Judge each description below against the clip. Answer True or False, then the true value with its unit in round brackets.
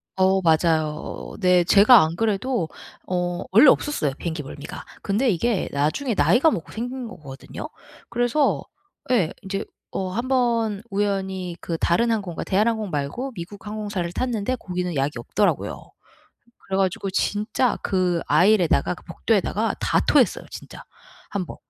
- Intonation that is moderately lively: True (4.7 semitones)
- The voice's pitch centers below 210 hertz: True (195 Hz)